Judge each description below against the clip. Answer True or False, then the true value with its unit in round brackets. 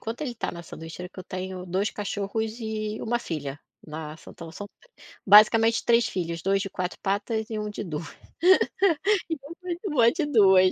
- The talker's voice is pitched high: True (210 Hz)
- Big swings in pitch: False (4.0 semitones)